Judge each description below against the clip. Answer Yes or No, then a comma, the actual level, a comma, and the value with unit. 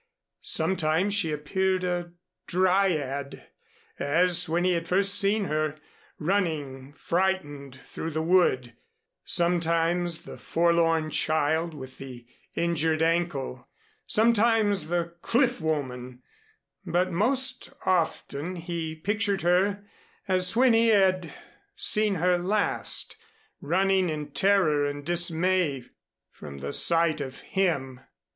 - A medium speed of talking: No, slow, 110 wpm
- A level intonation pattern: No, average, 3.7 semitones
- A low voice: No, medium, 170 Hz